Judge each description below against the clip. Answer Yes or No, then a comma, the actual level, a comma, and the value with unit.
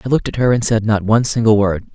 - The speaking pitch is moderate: No, low, 110 Hz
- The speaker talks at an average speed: No, fast, 310 wpm